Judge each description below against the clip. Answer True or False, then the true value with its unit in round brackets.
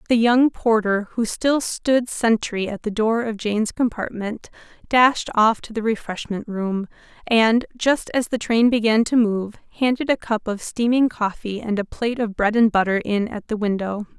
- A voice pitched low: False (225 Hz)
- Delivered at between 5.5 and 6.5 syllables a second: False (4.6 syllables/s)